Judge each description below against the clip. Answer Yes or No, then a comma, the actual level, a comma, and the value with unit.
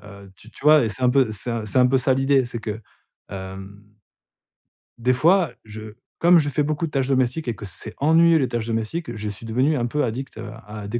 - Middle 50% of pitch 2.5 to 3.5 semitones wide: No, average, 4.6 semitones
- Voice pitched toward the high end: No, low, 120 Hz